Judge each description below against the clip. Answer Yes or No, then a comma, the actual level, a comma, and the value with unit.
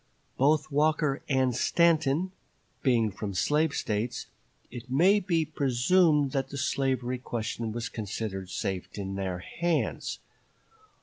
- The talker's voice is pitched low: Yes, low, 130 Hz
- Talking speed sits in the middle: No, slow, 120 wpm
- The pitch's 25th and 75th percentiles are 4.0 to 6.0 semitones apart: Yes, average, 5.3 semitones